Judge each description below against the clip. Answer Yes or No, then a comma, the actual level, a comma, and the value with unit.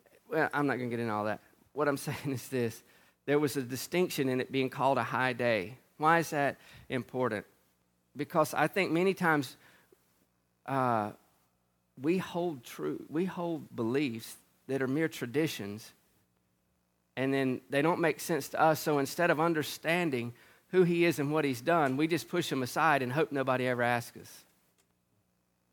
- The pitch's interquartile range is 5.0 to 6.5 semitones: Yes, wide, 5.6 semitones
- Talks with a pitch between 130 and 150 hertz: Yes, low, 135 Hz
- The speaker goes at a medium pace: Yes, average, 175 wpm